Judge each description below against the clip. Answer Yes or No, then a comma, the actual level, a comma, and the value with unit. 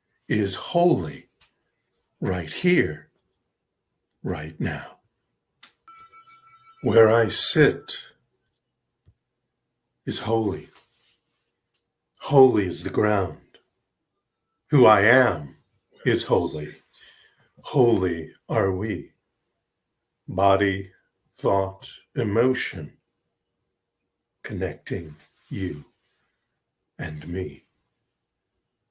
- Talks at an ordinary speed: No, slow, 60 wpm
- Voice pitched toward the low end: Yes, low, 110 Hz